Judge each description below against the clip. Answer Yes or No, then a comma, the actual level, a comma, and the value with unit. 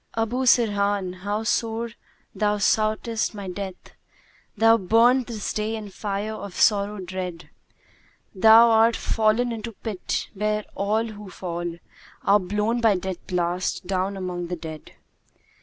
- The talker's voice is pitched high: Yes, high, 210 Hz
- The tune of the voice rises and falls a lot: No, average, 3.0 semitones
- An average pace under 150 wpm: Yes, average, 140 wpm